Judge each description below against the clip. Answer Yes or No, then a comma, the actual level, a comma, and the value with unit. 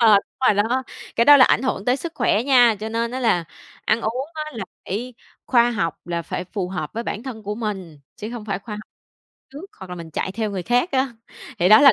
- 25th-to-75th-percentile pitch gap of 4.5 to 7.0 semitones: No, average, 4.0 semitones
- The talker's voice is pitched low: No, high, 220 Hz